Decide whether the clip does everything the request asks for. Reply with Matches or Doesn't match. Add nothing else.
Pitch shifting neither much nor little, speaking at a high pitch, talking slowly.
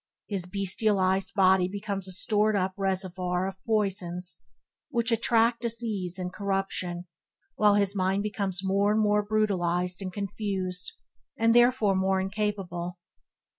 Doesn't match